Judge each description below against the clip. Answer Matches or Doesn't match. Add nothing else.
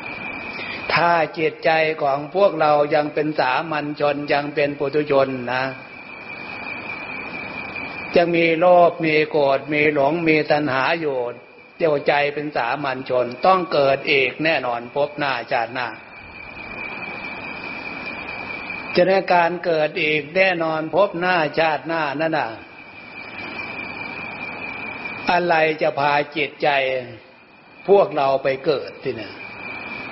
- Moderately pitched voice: Matches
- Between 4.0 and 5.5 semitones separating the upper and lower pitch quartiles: Doesn't match